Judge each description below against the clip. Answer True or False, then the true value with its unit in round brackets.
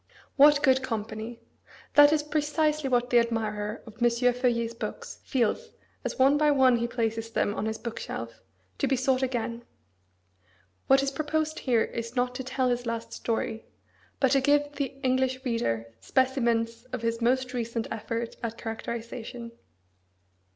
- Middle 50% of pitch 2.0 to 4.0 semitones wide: True (2.6 semitones)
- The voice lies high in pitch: True (245 Hz)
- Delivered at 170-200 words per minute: False (160 wpm)